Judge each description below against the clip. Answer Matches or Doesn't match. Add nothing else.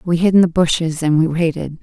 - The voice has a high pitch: Doesn't match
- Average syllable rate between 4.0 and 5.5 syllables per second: Doesn't match